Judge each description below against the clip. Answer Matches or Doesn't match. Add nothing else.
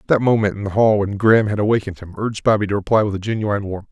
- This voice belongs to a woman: Doesn't match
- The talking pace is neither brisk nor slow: Doesn't match